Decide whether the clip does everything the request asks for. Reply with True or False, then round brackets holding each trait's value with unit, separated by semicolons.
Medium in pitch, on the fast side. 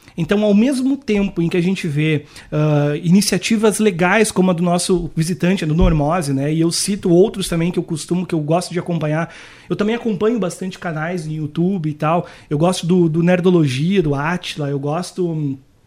True (175 Hz; 195 wpm)